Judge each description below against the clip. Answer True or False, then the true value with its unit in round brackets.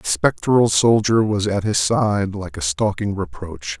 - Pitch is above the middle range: False (100 Hz)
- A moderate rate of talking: True (175 wpm)